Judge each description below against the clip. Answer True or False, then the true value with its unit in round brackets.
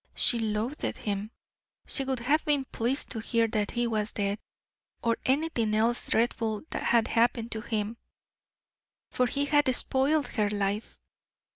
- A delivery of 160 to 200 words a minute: False (145 wpm)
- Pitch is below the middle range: False (230 Hz)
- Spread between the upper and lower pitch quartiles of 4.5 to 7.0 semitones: False (3.5 semitones)